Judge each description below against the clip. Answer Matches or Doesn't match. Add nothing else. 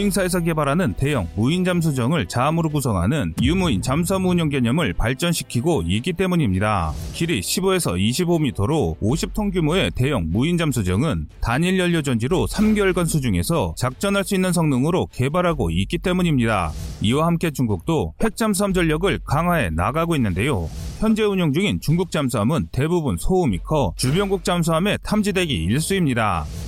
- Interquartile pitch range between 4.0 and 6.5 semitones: Doesn't match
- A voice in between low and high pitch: Matches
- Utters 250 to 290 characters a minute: Doesn't match